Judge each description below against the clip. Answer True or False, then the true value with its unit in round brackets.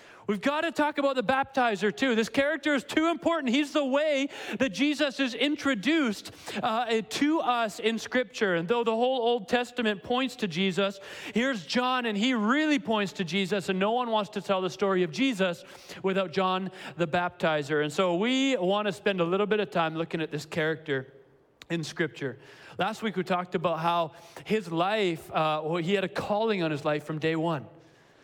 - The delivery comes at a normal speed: False (200 wpm)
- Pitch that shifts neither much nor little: False (6.3 semitones)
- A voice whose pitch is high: True (205 Hz)